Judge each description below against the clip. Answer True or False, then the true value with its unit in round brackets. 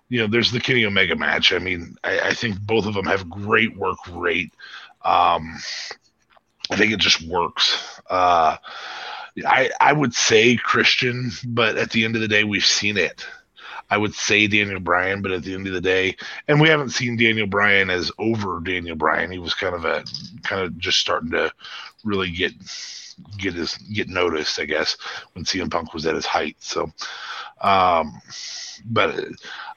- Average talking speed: True (185 wpm)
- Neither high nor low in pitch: False (105 Hz)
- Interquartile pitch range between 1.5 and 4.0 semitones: True (3.4 semitones)